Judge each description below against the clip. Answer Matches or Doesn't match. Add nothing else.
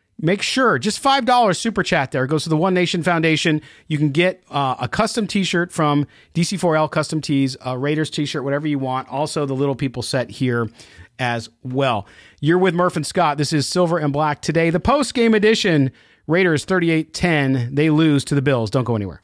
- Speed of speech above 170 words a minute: Matches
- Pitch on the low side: Doesn't match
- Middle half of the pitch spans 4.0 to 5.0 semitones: Matches